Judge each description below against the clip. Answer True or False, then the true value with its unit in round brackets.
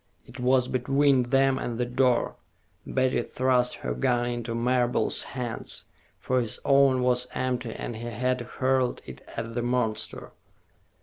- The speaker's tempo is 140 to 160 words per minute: True (145 wpm)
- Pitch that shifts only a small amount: True (1.3 semitones)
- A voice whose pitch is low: True (125 Hz)